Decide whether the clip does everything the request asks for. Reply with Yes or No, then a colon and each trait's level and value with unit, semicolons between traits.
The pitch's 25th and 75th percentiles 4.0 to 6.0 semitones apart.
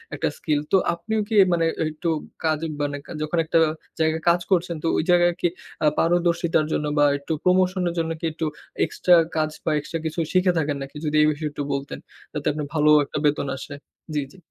No: narrow, 2.6 semitones